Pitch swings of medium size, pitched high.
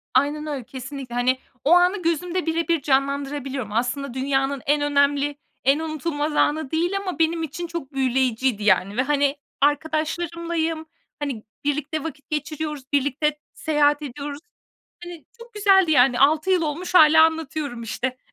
Yes: average, 3.0 semitones; very high, 290 Hz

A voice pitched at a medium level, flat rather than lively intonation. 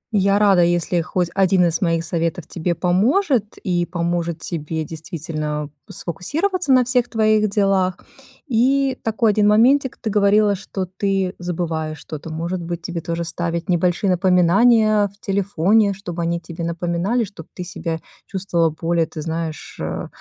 No: medium, 180 Hz; average, 3.7 semitones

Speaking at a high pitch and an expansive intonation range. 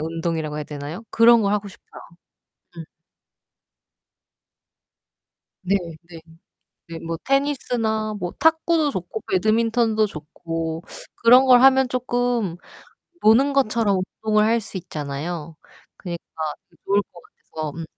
Yes: high, 200 Hz; wide, 6.2 semitones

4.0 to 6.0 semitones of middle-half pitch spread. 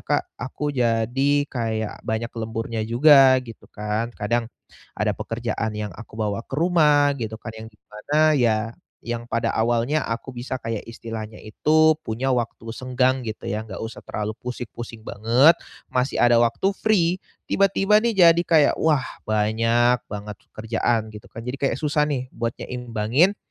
Yes: average, 4.3 semitones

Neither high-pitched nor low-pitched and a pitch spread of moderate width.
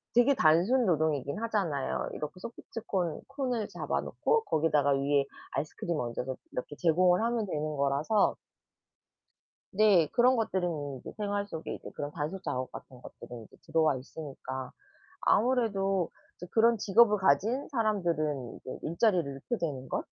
No: medium, 170 Hz; wide, 6.9 semitones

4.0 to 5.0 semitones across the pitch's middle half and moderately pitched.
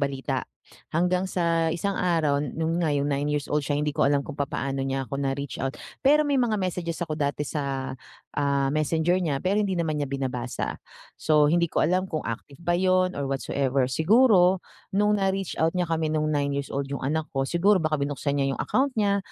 Yes: average, 4.4 semitones; medium, 155 Hz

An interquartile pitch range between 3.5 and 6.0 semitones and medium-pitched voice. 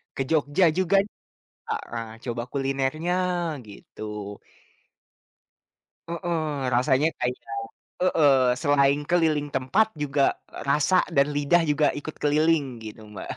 No: average, 2.8 semitones; medium, 145 Hz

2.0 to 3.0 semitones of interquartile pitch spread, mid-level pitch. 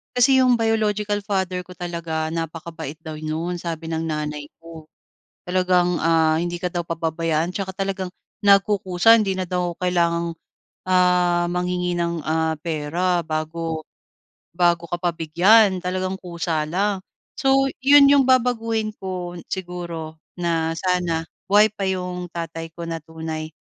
Yes: narrow, 2.6 semitones; medium, 175 Hz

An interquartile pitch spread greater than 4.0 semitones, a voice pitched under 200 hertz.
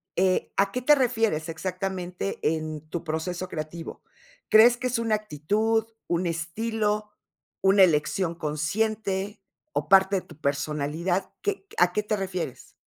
Yes: average, 4.6 semitones; high, 190 Hz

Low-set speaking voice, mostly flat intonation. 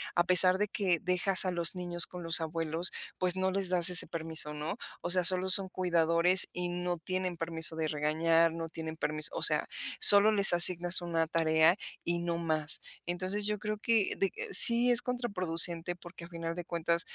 No: medium, 175 Hz; narrow, 2.0 semitones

